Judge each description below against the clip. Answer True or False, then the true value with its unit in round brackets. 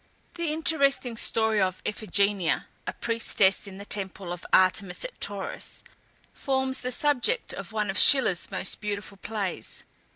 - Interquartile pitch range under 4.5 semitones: False (5.3 semitones)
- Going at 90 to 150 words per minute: True (140 wpm)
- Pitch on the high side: True (210 Hz)